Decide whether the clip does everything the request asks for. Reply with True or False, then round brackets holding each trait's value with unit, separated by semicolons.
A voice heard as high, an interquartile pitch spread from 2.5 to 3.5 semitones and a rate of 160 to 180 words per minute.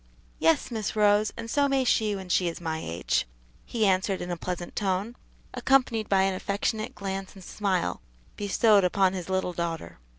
True (195 Hz; 3.1 semitones; 175 wpm)